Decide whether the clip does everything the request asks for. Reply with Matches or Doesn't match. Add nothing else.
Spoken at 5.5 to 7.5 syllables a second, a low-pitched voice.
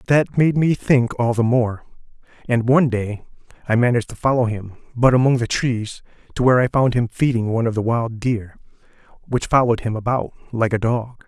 Matches